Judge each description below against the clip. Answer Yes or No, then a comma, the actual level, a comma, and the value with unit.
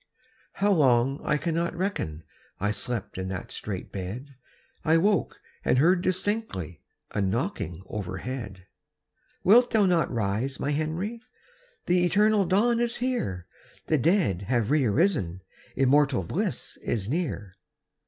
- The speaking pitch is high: No, medium, 140 Hz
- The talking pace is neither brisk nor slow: No, slow, 130 wpm